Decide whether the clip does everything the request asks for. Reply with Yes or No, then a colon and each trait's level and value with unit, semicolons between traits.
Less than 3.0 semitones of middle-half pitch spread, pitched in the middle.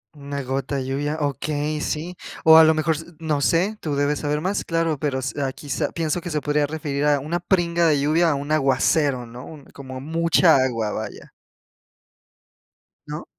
Yes: narrow, 2.6 semitones; medium, 150 Hz